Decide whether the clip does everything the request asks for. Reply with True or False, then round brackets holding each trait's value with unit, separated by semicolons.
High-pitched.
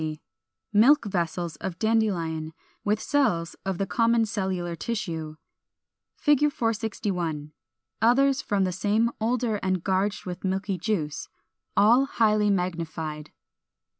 True (195 Hz)